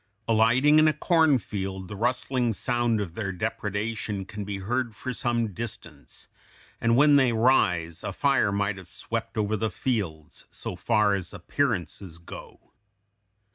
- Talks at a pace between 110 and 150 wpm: Yes, average, 145 wpm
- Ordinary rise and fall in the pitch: Yes, average, 3.9 semitones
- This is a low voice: Yes, low, 110 Hz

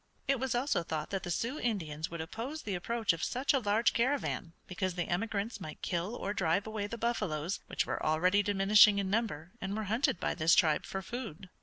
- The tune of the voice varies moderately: Yes, average, 4.9 semitones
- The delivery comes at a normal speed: No, fast, 210 wpm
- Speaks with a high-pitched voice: Yes, high, 200 Hz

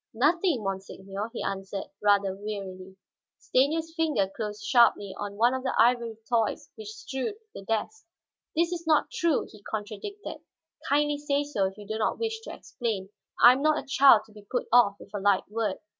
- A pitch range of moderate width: No, wide, 6.2 semitones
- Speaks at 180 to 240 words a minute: Yes, average, 185 wpm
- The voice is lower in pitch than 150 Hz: No, high, 225 Hz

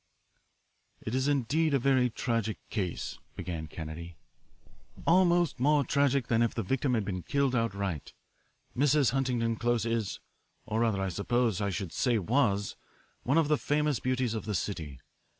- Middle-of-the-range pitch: No, low, 115 Hz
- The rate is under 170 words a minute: Yes, average, 155 wpm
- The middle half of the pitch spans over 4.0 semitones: Yes, average, 5.3 semitones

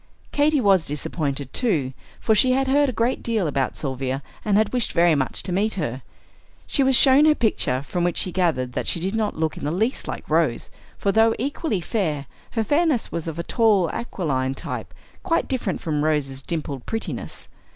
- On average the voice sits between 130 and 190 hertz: Yes, medium, 185 Hz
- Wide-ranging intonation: Yes, wide, 7.8 semitones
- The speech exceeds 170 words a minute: Yes, average, 195 wpm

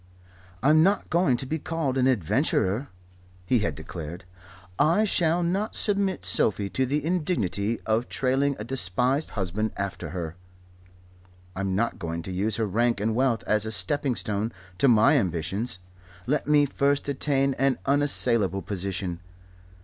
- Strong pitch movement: Yes, wide, 6.4 semitones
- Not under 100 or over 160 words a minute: Yes, average, 150 wpm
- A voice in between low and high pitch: No, low, 120 Hz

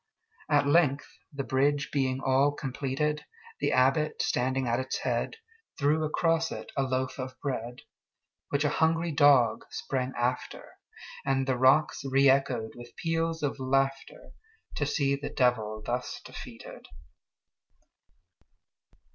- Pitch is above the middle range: No, low, 135 Hz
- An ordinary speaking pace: No, slow, 110 wpm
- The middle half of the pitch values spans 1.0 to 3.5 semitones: Yes, average, 2.7 semitones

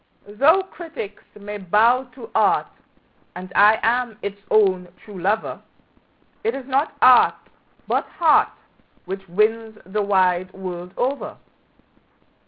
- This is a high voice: Yes, high, 210 Hz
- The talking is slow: Yes, slow, 120 wpm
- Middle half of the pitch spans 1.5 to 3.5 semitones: No, average, 4.9 semitones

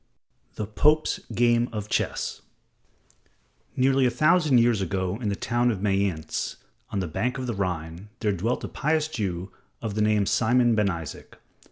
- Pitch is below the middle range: Yes, low, 110 Hz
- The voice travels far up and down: No, average, 4.1 semitones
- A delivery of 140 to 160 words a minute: No, average, 170 wpm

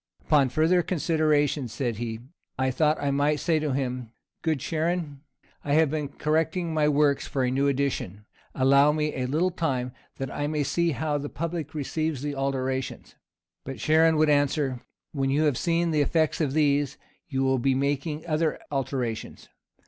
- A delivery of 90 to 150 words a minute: No, average, 175 wpm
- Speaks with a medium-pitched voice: Yes, medium, 145 Hz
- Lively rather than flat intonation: No, average, 2.7 semitones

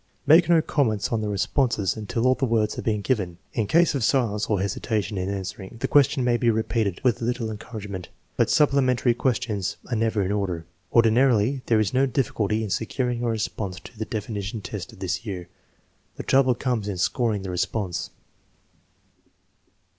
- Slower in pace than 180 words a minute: No, average, 190 wpm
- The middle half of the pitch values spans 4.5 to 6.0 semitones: No, average, 3.6 semitones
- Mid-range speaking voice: No, low, 110 Hz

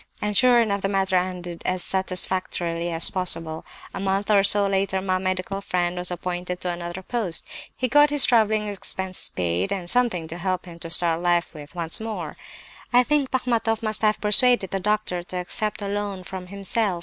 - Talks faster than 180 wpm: Yes, average, 190 wpm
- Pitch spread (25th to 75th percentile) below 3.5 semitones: Yes, average, 3.1 semitones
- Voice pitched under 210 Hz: Yes, high, 190 Hz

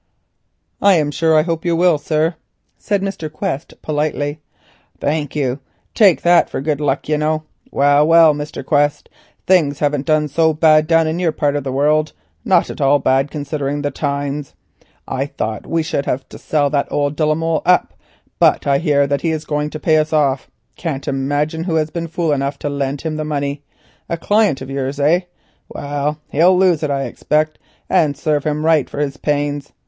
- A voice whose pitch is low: No, medium, 150 Hz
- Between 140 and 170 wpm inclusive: No, average, 200 wpm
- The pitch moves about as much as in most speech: No, narrow, 2.0 semitones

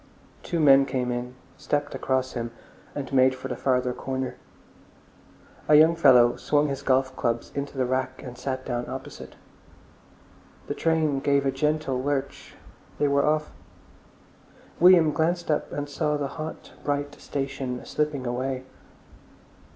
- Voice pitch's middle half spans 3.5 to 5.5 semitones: No, narrow, 2.4 semitones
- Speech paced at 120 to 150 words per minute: Yes, average, 145 wpm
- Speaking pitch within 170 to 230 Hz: No, low, 135 Hz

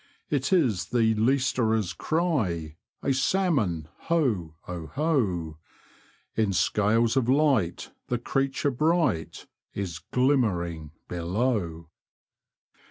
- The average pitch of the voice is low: Yes, low, 110 Hz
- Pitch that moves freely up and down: Yes, wide, 7.8 semitones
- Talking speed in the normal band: No, slow, 90 wpm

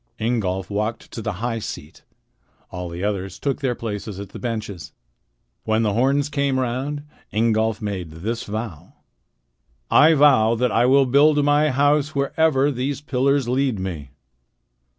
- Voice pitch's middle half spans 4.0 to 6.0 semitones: Yes, average, 5.1 semitones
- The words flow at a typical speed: Yes, average, 150 wpm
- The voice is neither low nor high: No, low, 120 Hz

